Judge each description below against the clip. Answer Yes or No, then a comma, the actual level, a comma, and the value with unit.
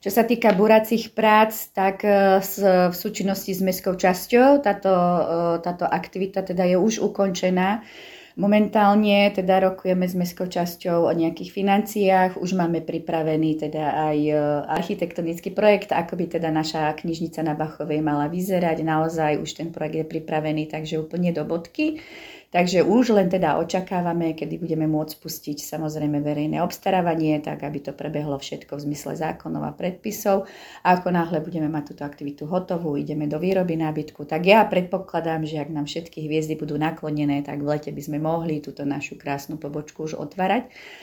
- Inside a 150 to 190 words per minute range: Yes, average, 160 wpm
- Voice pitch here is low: No, medium, 170 Hz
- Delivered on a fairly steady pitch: No, average, 3.9 semitones